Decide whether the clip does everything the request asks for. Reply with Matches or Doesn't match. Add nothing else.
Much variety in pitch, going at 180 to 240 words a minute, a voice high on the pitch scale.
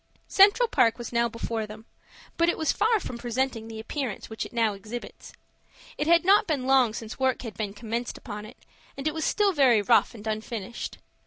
Doesn't match